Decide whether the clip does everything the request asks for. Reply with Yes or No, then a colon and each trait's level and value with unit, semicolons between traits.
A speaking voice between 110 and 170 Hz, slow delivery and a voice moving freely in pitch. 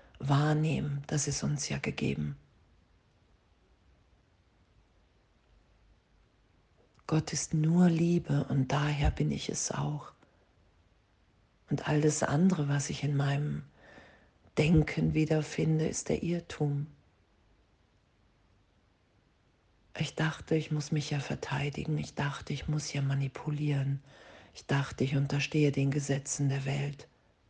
Yes: medium, 140 Hz; slow, 105 wpm; wide, 7.5 semitones